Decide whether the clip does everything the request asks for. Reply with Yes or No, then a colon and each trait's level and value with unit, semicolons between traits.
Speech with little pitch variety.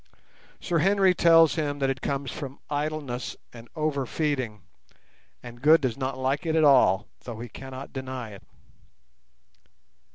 No: average, 3.4 semitones